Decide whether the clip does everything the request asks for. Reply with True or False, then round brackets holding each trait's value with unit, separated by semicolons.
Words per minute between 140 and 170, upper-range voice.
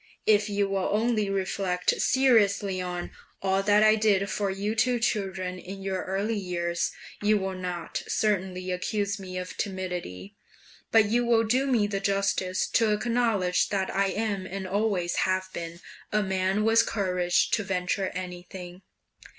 True (155 wpm; 195 Hz)